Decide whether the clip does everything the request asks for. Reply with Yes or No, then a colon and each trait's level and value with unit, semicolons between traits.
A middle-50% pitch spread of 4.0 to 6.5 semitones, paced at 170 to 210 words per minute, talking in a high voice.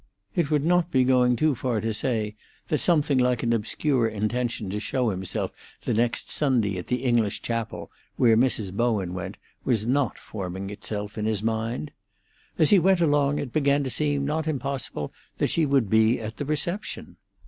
No: average, 4.8 semitones; average, 180 wpm; low, 120 Hz